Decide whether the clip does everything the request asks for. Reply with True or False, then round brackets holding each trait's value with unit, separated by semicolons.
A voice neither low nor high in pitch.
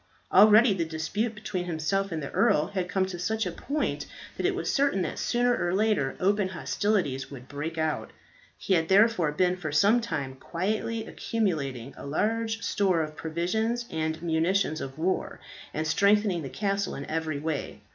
True (180 Hz)